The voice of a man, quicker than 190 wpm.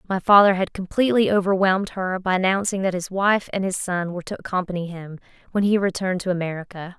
No: female; average, 200 wpm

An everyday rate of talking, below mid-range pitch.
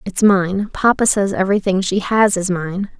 No: average, 180 wpm; high, 195 Hz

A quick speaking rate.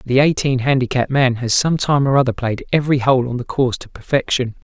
Yes: fast, 230 wpm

